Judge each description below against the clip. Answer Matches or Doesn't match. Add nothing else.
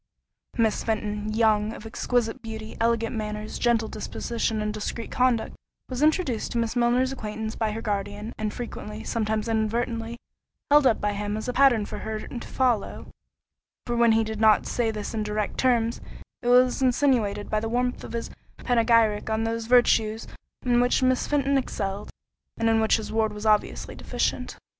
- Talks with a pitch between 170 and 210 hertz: Doesn't match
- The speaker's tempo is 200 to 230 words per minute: Doesn't match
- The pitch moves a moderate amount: Doesn't match